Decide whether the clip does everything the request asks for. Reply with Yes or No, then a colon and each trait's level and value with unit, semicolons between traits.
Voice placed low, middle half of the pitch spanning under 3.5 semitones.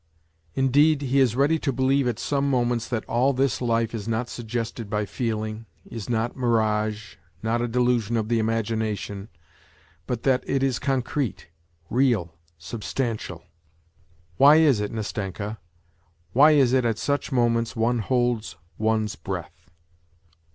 Yes: low, 115 Hz; average, 3.1 semitones